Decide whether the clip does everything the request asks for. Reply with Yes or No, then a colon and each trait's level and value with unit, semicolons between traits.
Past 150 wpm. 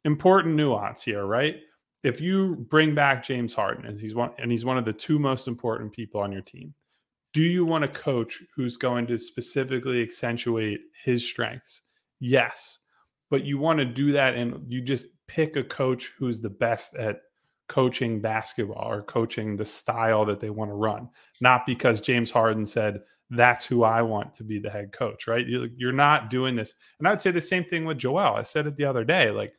Yes: fast, 205 wpm